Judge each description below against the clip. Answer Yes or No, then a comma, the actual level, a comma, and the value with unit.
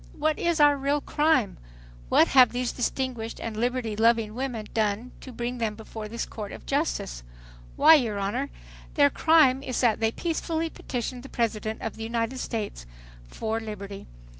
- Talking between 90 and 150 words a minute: No, average, 165 wpm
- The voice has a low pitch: No, high, 235 Hz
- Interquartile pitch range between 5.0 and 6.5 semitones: No, average, 3.6 semitones